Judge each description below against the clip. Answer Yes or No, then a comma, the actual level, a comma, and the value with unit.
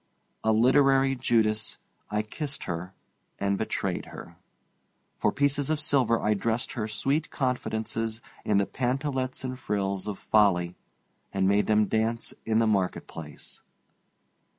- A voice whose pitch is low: Yes, low, 110 Hz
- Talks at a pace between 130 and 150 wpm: Yes, slow, 135 wpm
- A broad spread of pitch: No, average, 4.1 semitones